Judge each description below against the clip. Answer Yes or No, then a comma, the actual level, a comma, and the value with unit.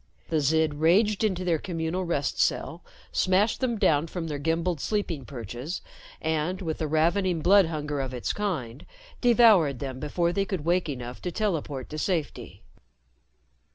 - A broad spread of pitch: No, average, 4.1 semitones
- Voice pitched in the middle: Yes, medium, 165 Hz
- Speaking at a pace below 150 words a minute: No, average, 155 wpm